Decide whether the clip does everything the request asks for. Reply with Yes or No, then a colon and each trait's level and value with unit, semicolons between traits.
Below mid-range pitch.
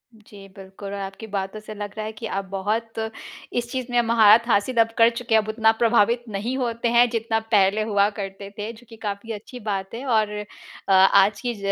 No: high, 215 Hz